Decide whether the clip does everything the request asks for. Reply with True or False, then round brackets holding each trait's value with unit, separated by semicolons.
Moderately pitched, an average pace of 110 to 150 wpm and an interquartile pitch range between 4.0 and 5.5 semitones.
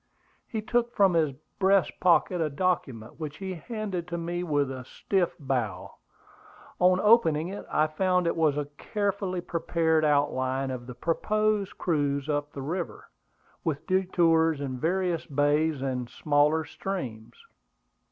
True (160 Hz; 140 wpm; 4.4 semitones)